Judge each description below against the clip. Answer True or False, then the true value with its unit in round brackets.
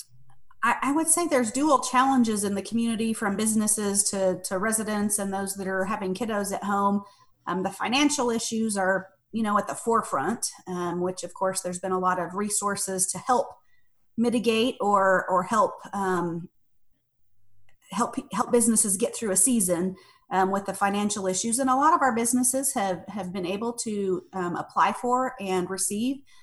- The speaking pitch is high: True (200 Hz)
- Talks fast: False (175 wpm)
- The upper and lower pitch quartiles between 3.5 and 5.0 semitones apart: True (4.0 semitones)